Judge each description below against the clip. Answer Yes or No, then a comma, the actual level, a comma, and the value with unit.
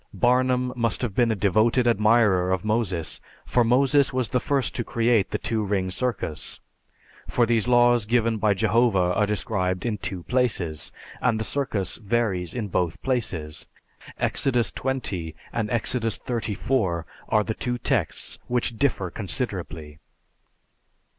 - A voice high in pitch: No, low, 110 Hz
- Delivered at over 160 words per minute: No, average, 140 wpm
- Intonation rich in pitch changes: No, average, 4.3 semitones